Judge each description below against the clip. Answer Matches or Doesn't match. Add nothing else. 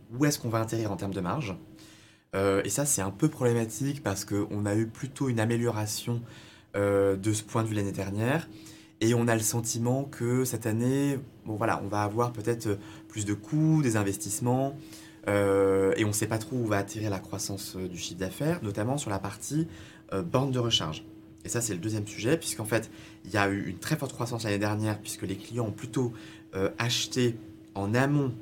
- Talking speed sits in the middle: Matches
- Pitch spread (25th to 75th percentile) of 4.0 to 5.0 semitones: Doesn't match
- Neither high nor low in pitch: Doesn't match